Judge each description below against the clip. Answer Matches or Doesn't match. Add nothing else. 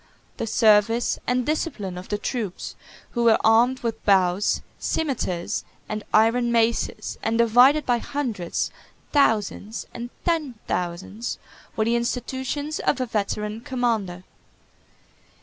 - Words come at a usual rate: Doesn't match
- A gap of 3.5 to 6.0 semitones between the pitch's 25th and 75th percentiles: Doesn't match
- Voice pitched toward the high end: Matches